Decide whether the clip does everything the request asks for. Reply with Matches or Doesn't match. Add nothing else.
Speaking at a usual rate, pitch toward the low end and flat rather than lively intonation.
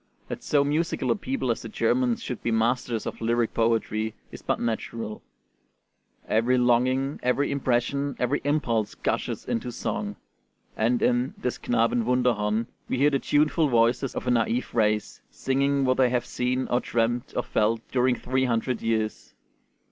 Matches